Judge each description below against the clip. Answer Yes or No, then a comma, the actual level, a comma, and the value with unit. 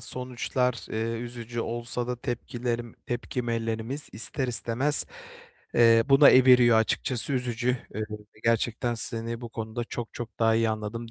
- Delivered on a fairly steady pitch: Yes, narrow, 1.5 semitones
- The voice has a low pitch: Yes, low, 120 Hz